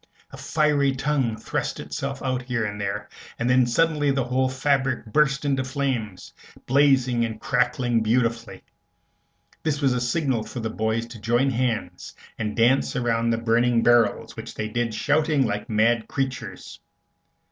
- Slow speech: No, average, 150 wpm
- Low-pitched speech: Yes, low, 125 Hz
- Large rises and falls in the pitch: No, average, 3.0 semitones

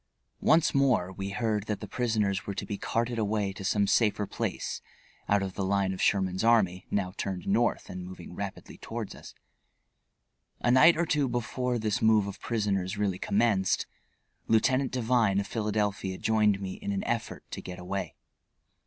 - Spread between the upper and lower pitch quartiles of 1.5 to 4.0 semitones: Yes, average, 3.1 semitones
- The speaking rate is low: No, average, 170 wpm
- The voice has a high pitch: No, low, 105 Hz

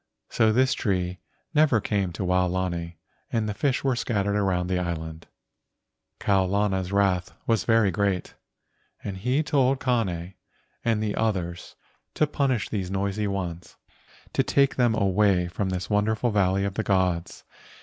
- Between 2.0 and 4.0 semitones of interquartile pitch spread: Yes, average, 3.4 semitones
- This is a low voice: Yes, low, 100 Hz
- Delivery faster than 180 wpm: No, average, 150 wpm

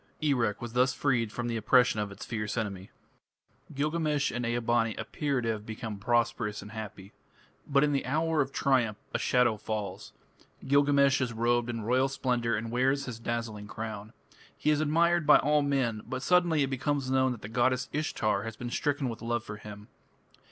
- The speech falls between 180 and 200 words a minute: Yes, average, 185 wpm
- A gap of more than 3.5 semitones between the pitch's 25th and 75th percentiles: Yes, average, 3.9 semitones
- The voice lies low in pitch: Yes, low, 120 Hz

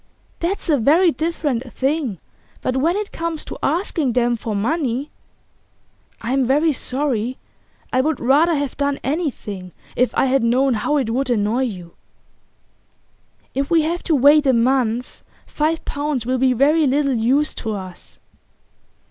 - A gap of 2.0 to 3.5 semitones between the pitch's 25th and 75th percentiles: No, average, 4.0 semitones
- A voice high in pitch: Yes, very high, 270 Hz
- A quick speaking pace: No, average, 155 wpm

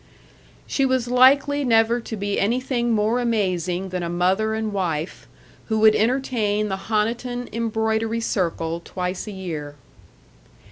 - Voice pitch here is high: Yes, high, 220 Hz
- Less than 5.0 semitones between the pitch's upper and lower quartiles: Yes, average, 4.1 semitones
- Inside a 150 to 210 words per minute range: No, slow, 135 wpm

